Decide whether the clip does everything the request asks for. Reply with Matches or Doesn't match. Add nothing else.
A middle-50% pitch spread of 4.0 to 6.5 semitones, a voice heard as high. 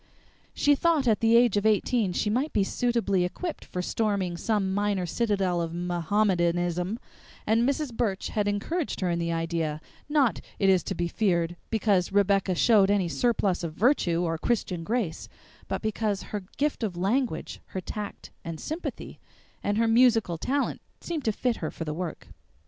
Matches